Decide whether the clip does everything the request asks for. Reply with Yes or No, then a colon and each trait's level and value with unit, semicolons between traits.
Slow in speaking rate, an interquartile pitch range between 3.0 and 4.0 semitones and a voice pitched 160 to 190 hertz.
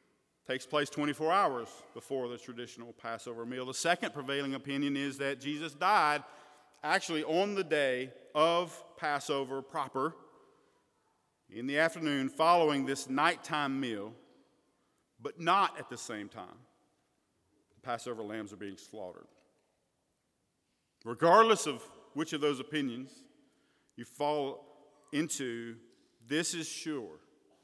No: slow, 120 wpm; average, 3.5 semitones; medium, 145 Hz